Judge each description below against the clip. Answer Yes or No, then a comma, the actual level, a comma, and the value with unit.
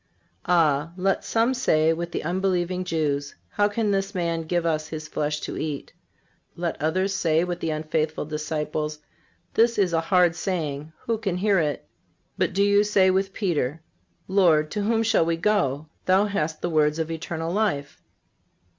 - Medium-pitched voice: Yes, medium, 170 Hz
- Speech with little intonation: No, average, 3.9 semitones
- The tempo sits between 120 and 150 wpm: No, average, 170 wpm